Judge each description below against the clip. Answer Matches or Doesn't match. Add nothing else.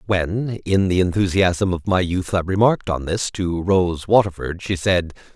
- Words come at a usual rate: Matches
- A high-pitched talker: Doesn't match